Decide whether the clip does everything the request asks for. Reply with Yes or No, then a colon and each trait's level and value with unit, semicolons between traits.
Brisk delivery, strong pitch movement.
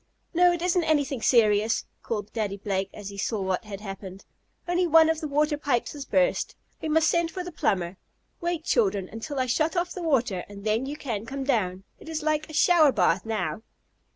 Yes: fast, 210 wpm; wide, 7.5 semitones